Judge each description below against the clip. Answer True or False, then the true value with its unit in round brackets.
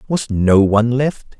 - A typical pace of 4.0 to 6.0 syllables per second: True (4.1 syllables/s)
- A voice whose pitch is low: True (120 Hz)